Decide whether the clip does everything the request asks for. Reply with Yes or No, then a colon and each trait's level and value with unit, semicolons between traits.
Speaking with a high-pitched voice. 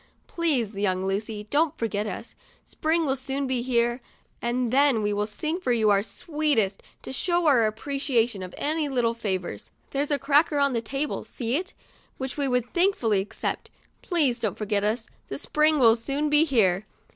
Yes: high, 245 Hz